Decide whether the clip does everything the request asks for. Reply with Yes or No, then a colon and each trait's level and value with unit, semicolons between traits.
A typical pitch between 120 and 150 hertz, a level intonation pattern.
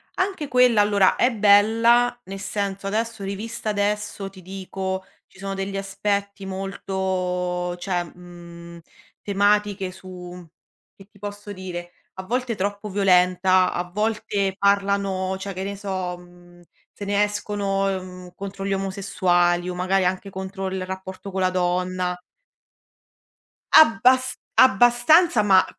No: high, 195 Hz; narrow, 1.9 semitones